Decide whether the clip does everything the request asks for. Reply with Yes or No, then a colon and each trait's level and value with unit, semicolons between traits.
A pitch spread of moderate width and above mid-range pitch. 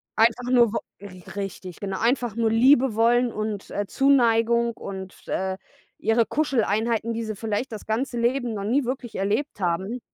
Yes: average, 3.0 semitones; high, 225 Hz